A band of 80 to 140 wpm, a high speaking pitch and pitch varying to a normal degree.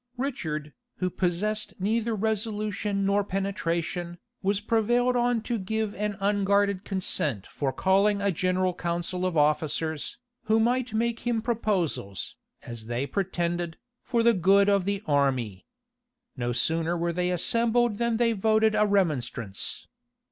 Yes: slow, 135 wpm; high, 195 Hz; average, 4.3 semitones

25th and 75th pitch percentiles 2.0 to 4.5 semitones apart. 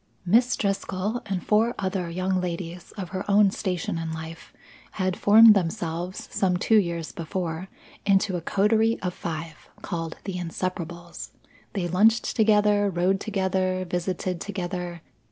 Yes: average, 2.7 semitones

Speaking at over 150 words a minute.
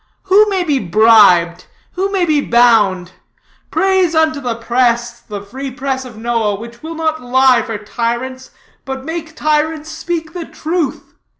Yes: average, 160 wpm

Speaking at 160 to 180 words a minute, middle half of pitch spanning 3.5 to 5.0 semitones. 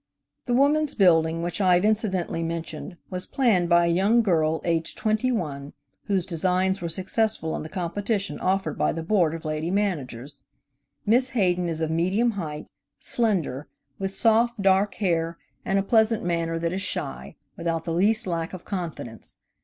Yes: average, 170 wpm; average, 3.9 semitones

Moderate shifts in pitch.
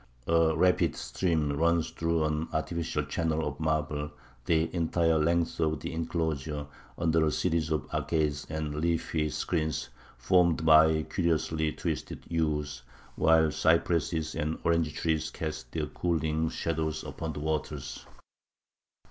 No: narrow, 1.3 semitones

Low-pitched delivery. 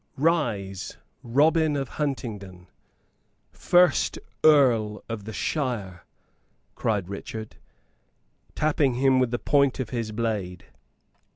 Yes: low, 120 Hz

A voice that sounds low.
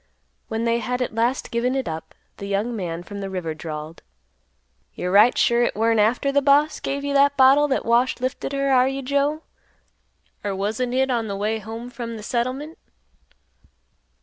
No: high, 240 Hz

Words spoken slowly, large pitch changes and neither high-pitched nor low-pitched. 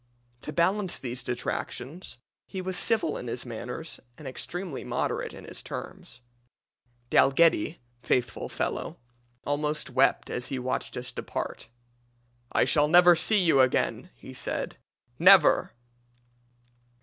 Yes: slow, 125 wpm; wide, 5.7 semitones; medium, 150 Hz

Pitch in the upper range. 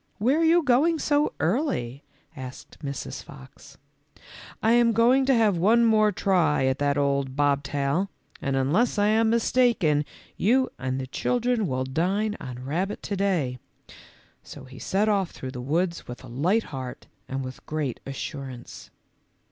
No: medium, 170 Hz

